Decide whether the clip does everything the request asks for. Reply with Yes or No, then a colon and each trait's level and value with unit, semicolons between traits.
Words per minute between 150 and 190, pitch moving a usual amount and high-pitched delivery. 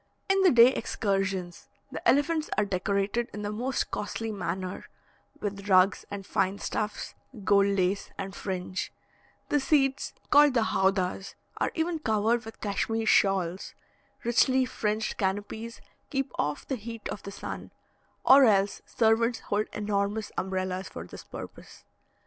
No: average, 140 wpm; average, 3.4 semitones; high, 210 Hz